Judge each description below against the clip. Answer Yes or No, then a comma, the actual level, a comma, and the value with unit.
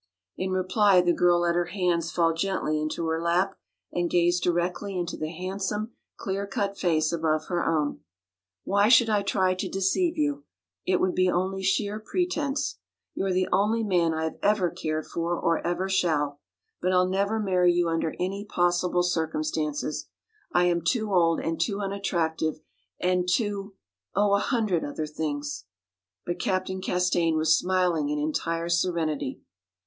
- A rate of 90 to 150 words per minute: No, average, 165 wpm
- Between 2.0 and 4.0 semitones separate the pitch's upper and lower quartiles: Yes, average, 2.9 semitones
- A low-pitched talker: No, medium, 180 Hz